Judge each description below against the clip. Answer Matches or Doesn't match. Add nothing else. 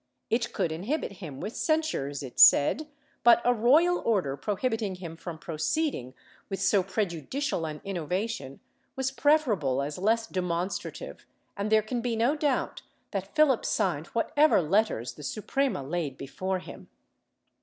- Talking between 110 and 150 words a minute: Matches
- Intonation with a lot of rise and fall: Matches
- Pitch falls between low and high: Doesn't match